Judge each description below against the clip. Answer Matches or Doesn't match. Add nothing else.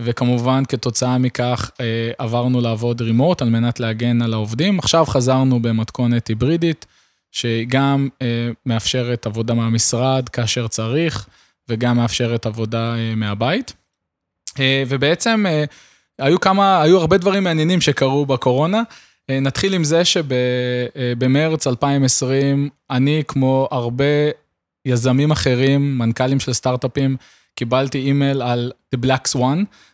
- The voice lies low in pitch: Matches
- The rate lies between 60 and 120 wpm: Matches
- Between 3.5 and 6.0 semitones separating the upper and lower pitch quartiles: Doesn't match